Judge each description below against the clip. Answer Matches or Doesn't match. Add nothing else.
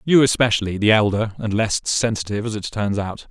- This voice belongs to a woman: Doesn't match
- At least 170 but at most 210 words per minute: Matches